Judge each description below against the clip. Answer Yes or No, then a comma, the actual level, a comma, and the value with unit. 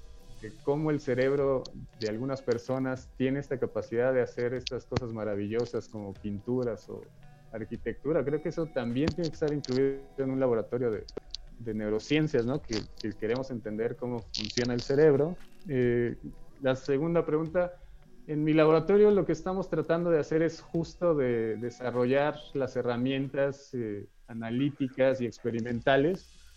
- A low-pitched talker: Yes, low, 130 Hz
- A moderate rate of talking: Yes, average, 145 wpm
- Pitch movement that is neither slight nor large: Yes, average, 4.1 semitones